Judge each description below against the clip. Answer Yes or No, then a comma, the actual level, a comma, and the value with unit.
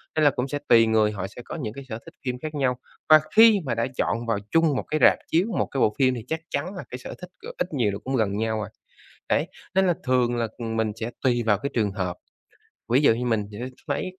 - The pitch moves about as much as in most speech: Yes, average, 4.4 semitones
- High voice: No, low, 125 Hz